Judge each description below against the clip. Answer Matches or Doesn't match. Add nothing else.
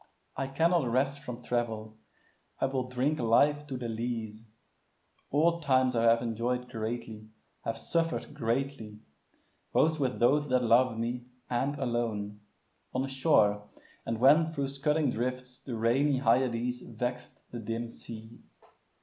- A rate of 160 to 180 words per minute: Doesn't match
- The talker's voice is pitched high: Doesn't match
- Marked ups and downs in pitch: Doesn't match